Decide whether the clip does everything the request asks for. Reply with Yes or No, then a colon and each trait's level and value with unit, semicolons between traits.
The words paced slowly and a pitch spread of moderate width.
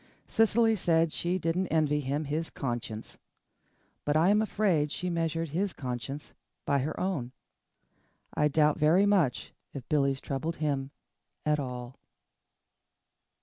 Yes: slow, 130 wpm; average, 3.8 semitones